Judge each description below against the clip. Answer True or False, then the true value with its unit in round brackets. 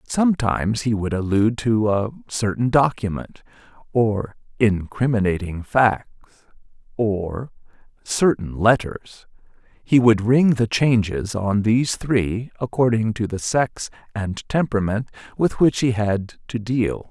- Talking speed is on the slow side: True (115 wpm)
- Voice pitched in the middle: False (110 Hz)